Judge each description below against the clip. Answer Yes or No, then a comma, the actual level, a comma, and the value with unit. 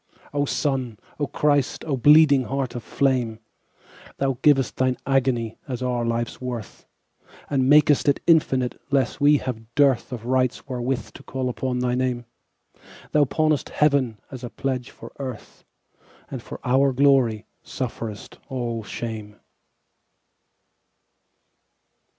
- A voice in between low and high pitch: No, low, 130 Hz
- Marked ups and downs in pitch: No, narrow, 2.5 semitones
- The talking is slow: Yes, slow, 115 wpm